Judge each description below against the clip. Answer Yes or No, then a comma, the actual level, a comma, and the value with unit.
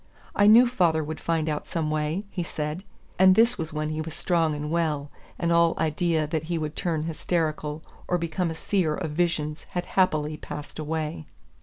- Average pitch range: No, narrow, 2.1 semitones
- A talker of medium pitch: Yes, medium, 160 Hz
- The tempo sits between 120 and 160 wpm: No, average, 190 wpm